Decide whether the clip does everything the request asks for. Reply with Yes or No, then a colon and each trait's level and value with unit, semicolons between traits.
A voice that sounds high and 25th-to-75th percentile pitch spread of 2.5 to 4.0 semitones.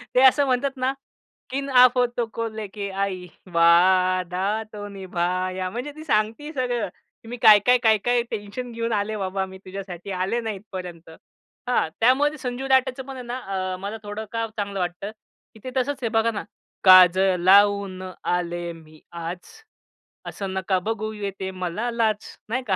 No: high, 205 Hz; average, 4.6 semitones